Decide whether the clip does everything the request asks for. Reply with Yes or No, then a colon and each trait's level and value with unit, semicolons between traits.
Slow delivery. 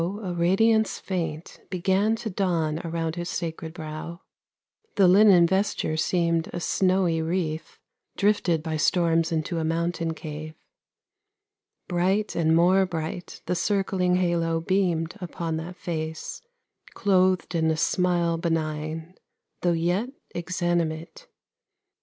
Yes: slow, 115 wpm